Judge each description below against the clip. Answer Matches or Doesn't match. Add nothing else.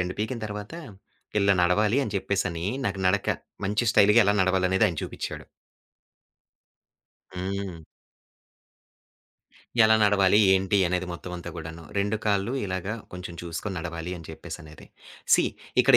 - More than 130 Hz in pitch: Doesn't match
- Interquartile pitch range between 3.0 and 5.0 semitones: Doesn't match